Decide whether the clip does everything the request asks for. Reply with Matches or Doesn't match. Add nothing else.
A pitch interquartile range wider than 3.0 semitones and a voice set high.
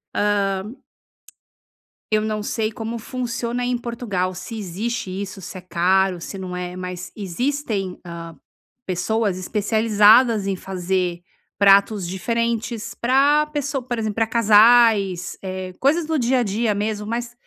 Matches